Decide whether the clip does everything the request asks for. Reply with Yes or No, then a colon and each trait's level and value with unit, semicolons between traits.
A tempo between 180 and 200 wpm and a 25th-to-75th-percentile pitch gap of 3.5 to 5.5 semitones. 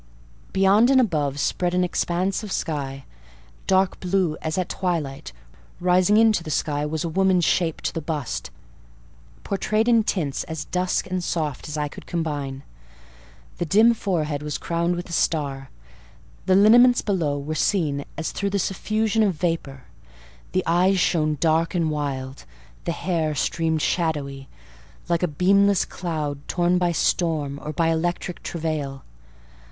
No: average, 150 wpm; average, 3.8 semitones